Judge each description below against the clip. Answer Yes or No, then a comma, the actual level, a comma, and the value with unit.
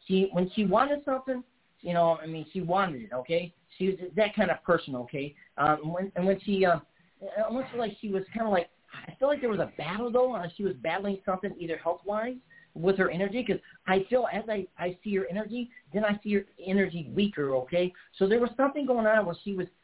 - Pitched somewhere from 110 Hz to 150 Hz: No, high, 195 Hz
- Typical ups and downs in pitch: Yes, average, 3.9 semitones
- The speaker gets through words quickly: Yes, fast, 225 wpm